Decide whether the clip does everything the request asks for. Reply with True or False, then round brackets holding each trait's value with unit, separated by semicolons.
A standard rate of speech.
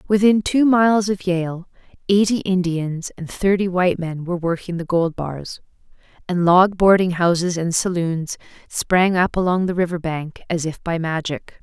True (165 wpm)